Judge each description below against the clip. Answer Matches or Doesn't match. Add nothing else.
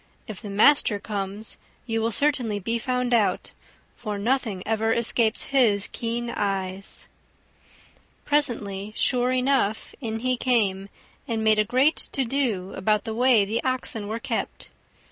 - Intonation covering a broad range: Doesn't match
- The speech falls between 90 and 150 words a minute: Matches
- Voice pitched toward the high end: Matches